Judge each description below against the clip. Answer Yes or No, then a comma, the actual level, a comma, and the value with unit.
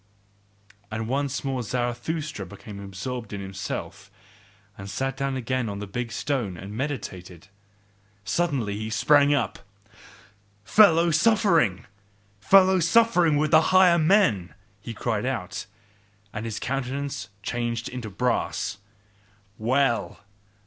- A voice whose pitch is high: No, low, 125 Hz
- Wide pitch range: Yes, wide, 6.0 semitones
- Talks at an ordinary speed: No, slow, 115 wpm